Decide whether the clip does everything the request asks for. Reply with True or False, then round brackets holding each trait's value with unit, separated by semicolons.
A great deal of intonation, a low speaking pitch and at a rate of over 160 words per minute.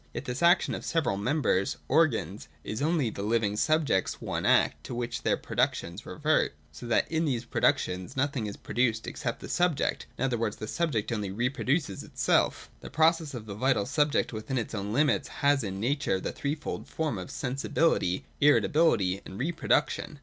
True (5.7 semitones; 125 Hz; 180 wpm)